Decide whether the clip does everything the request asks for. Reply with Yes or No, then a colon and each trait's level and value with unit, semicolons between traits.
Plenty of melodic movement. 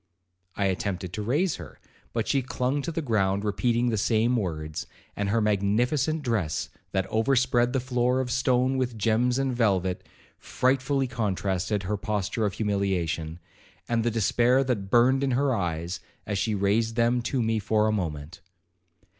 No: average, 4.2 semitones